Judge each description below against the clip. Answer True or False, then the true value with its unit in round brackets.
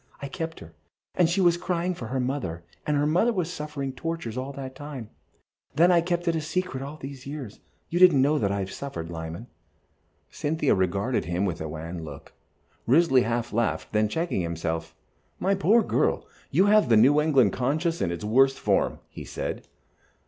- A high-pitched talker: False (135 Hz)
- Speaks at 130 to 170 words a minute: False (185 wpm)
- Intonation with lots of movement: True (7.8 semitones)